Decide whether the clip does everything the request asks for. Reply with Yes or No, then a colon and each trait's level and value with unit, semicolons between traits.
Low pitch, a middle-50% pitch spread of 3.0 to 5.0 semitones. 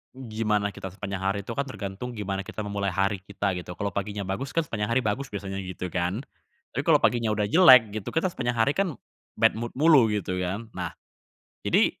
Yes: low, 105 Hz; average, 3.7 semitones